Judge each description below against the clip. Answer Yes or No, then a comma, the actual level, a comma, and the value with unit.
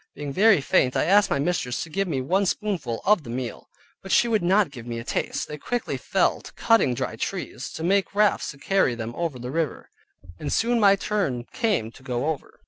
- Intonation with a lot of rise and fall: Yes, wide, 7.7 semitones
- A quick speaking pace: Yes, fast, 220 wpm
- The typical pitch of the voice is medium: Yes, medium, 160 Hz